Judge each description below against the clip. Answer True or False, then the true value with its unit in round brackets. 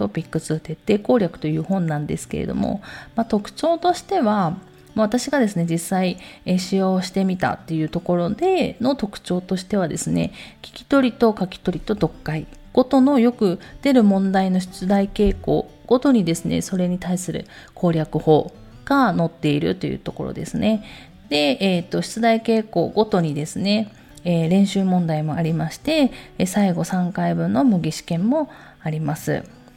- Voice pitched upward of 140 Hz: True (185 Hz)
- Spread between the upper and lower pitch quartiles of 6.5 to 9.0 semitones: False (5.1 semitones)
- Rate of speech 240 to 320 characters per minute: True (315 characters per minute)